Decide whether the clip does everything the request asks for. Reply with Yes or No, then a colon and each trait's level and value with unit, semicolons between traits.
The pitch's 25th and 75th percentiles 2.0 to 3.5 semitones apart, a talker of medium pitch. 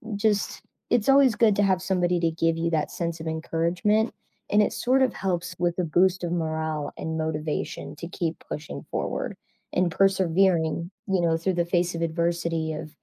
Yes: average, 2.8 semitones; medium, 170 Hz